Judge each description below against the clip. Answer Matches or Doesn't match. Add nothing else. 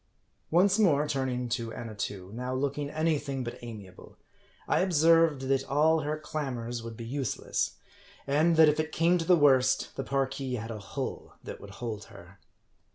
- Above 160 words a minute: Matches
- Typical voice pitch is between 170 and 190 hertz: Doesn't match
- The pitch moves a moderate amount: Matches